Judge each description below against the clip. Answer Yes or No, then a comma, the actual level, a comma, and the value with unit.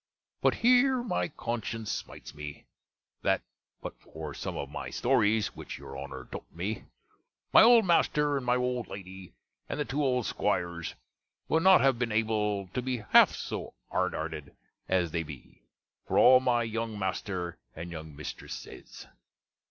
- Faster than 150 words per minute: Yes, average, 160 wpm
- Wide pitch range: Yes, wide, 7.0 semitones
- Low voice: Yes, low, 110 Hz